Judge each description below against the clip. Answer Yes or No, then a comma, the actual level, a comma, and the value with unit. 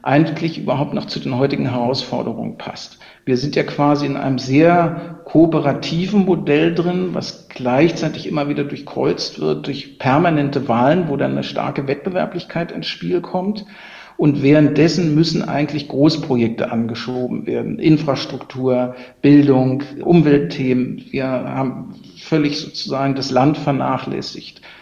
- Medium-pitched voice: Yes, medium, 145 Hz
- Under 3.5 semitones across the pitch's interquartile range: No, average, 4.0 semitones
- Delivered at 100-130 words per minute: Yes, slow, 125 wpm